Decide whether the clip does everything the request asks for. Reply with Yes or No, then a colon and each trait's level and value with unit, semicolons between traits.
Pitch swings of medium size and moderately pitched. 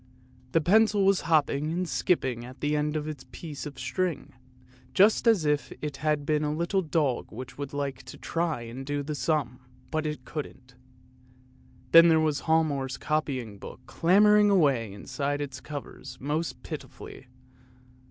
Yes: average, 3.3 semitones; medium, 150 Hz